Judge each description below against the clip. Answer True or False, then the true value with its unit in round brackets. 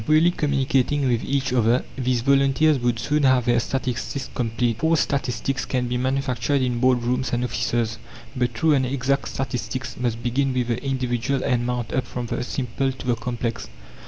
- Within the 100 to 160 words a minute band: False (180 wpm)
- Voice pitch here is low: True (125 Hz)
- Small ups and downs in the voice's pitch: True (2.1 semitones)